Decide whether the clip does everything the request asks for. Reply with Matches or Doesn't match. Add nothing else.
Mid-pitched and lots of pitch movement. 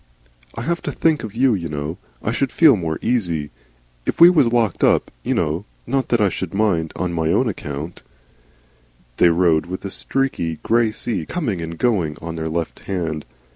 Doesn't match